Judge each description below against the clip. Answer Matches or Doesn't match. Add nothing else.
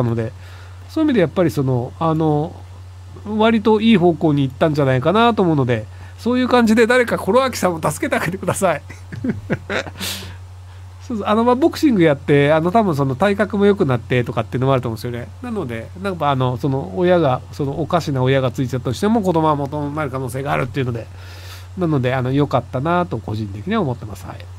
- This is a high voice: Doesn't match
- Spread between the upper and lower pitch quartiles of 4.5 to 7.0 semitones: Doesn't match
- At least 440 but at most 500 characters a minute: Matches